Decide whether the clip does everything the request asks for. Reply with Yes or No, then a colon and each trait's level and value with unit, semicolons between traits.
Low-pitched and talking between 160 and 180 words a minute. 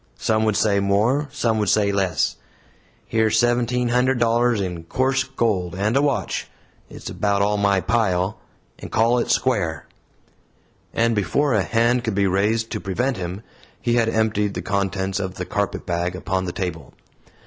Yes: low, 105 Hz; average, 165 wpm